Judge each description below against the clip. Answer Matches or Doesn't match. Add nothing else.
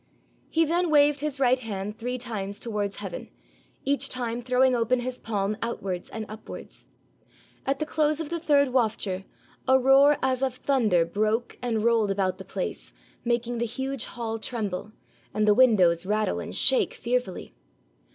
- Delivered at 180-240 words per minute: Doesn't match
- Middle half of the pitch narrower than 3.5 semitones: Doesn't match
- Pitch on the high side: Matches